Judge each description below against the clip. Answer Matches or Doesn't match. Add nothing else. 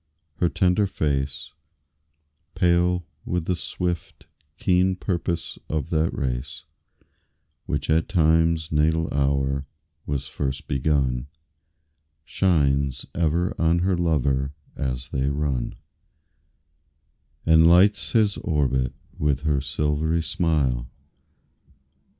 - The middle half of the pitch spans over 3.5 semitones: Matches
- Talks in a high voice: Doesn't match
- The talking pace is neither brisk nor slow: Doesn't match